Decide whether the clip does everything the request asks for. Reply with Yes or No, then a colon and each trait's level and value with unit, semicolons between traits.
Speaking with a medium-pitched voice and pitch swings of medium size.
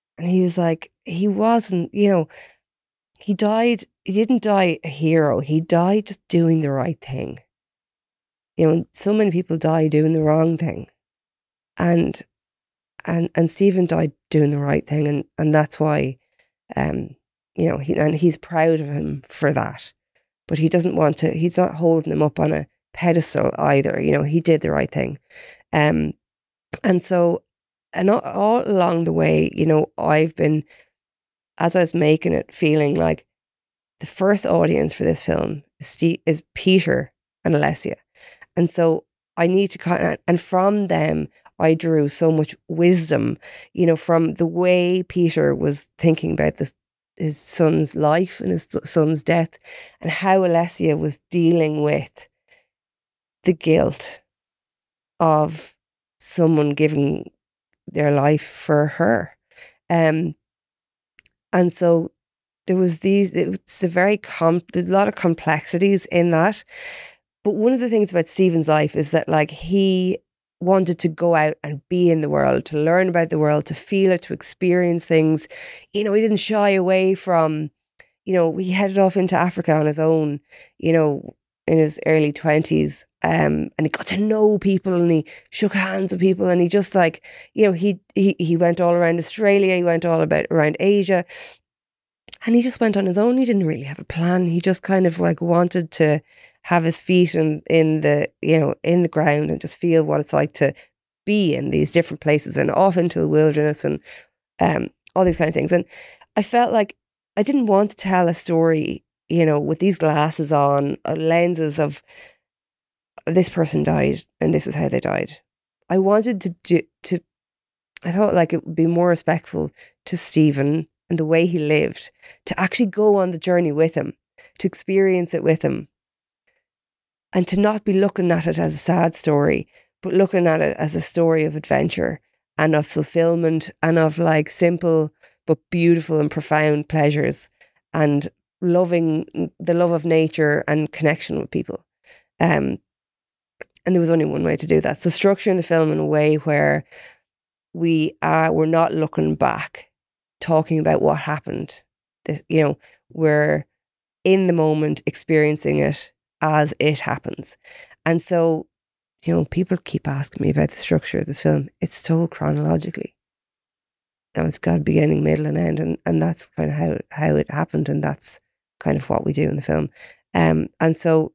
Yes: medium, 165 Hz; average, 3.0 semitones